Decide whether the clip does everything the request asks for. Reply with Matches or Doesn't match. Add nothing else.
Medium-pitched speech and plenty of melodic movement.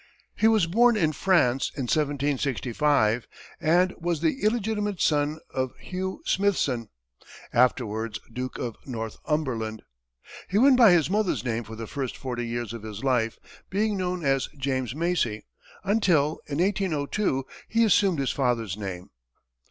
Matches